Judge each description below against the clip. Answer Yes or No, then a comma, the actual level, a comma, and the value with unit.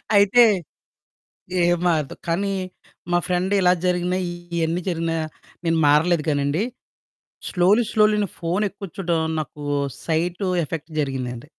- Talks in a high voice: No, medium, 175 Hz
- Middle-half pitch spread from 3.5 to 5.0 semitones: No, average, 2.9 semitones